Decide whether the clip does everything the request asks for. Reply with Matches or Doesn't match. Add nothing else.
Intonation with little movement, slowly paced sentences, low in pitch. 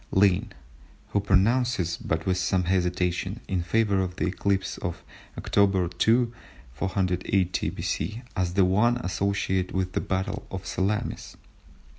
Matches